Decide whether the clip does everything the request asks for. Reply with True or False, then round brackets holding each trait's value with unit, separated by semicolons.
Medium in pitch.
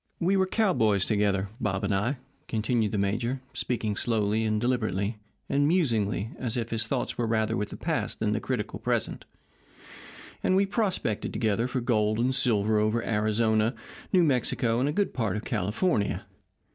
False (110 Hz)